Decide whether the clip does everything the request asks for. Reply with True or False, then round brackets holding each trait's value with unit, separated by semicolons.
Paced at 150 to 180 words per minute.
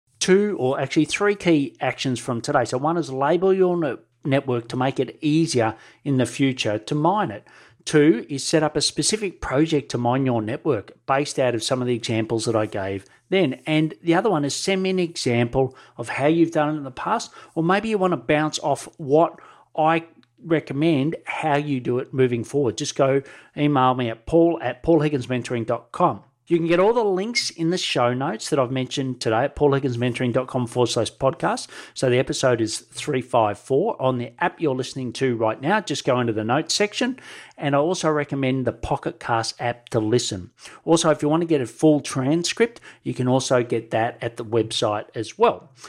False (200 wpm)